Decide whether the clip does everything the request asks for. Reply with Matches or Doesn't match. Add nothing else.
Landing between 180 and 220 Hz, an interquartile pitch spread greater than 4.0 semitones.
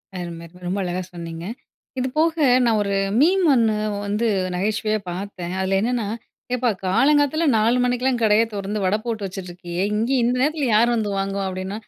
Matches